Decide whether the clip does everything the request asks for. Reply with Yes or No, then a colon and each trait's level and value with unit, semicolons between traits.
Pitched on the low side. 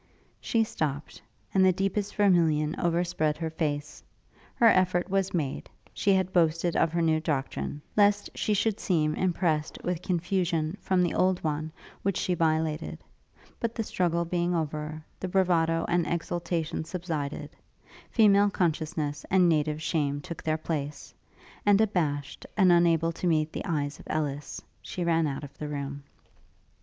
No: medium, 165 Hz